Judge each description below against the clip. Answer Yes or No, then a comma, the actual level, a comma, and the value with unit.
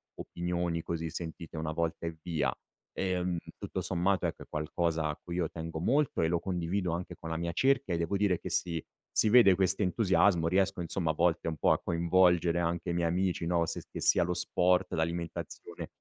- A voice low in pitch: Yes, very low, 85 Hz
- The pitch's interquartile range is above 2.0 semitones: No, narrow, 1.7 semitones